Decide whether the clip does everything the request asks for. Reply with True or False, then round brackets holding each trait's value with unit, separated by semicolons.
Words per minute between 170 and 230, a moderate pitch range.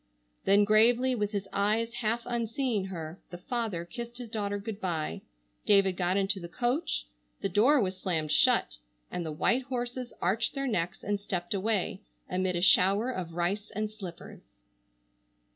False (160 wpm; 4.3 semitones)